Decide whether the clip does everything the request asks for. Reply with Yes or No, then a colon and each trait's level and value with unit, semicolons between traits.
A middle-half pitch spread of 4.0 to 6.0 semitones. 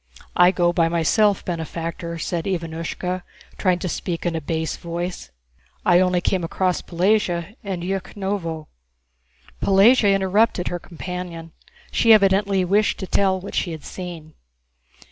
No: narrow, 2.5 semitones